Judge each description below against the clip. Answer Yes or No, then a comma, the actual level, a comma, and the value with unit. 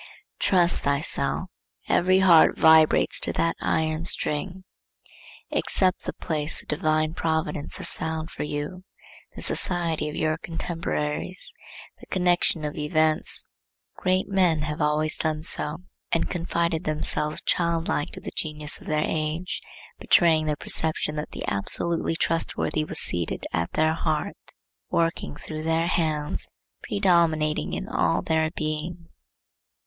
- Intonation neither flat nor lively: No, narrow, 1.8 semitones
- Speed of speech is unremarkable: No, slow, 130 wpm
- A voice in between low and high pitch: Yes, medium, 160 Hz